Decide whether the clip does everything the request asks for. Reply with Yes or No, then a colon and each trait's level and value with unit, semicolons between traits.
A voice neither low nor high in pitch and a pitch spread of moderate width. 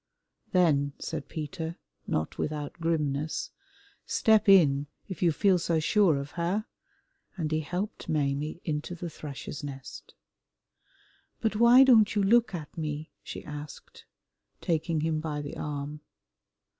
Yes: medium, 160 Hz; average, 3.6 semitones